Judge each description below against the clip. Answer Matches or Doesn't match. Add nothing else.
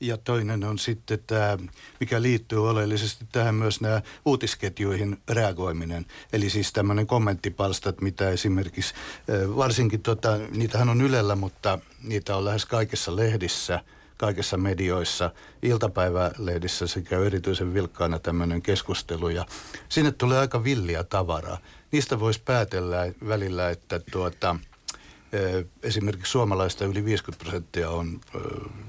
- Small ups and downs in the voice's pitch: Doesn't match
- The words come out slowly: Doesn't match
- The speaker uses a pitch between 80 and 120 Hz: Matches